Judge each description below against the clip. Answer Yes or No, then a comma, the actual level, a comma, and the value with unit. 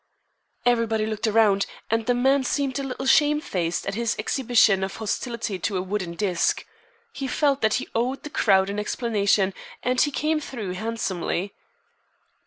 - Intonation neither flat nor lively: Yes, average, 4.6 semitones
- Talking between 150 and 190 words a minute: Yes, average, 160 wpm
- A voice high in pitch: Yes, high, 225 Hz